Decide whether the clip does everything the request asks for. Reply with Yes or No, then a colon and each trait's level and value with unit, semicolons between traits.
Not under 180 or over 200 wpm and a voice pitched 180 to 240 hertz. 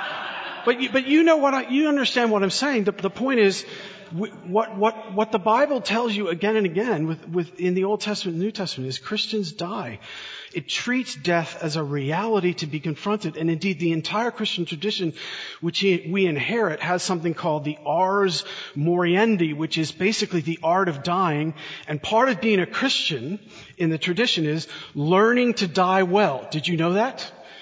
Yes: average, 190 wpm; high, 190 Hz